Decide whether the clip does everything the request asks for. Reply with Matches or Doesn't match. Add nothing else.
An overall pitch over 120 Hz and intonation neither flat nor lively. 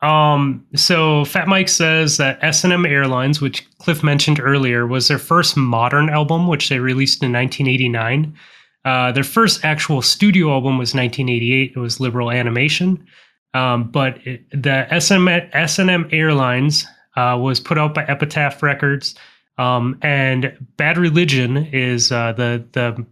Matches